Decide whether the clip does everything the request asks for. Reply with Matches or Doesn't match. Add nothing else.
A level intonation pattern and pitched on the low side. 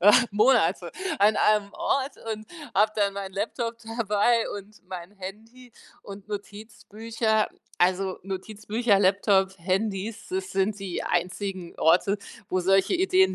Doesn't match